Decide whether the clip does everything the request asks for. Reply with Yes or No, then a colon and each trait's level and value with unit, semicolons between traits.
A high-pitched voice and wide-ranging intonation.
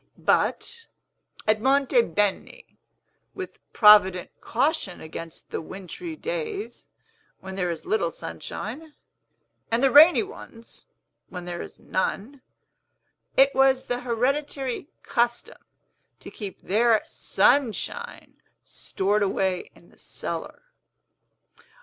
Yes: high, 240 Hz; wide, 7.0 semitones